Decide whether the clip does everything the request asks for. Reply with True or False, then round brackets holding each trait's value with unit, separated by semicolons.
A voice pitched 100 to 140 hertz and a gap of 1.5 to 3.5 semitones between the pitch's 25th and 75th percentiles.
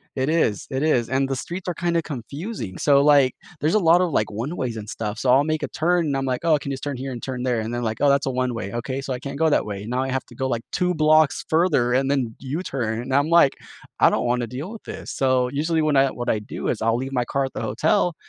False (135 Hz; 4.0 semitones)